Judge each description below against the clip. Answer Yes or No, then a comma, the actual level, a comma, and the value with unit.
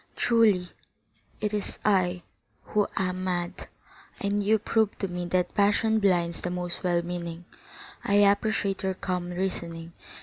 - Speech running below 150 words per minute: Yes, average, 140 wpm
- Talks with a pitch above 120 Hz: Yes, medium, 185 Hz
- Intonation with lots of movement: No, narrow, 2.5 semitones